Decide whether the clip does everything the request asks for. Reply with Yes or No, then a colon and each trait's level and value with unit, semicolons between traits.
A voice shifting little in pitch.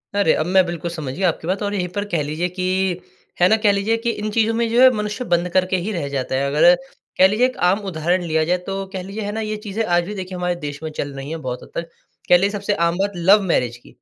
No: average, 3.5 semitones